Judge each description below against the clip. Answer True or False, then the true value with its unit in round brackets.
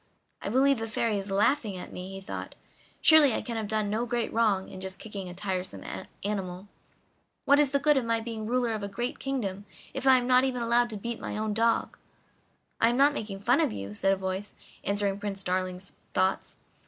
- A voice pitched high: True (215 Hz)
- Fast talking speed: True (215 wpm)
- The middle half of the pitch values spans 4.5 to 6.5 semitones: False (3.7 semitones)